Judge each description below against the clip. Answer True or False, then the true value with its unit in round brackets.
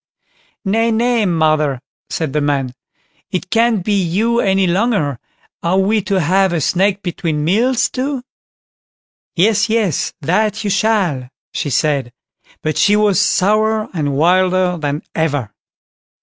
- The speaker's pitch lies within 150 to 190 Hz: True (185 Hz)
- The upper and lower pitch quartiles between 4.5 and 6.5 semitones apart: True (5.5 semitones)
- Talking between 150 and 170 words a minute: False (135 wpm)